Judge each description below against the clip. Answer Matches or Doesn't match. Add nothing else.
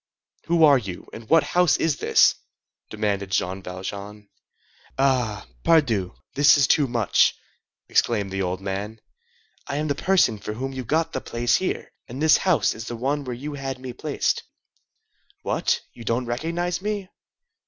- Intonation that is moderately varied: Doesn't match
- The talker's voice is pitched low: Matches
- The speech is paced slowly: Doesn't match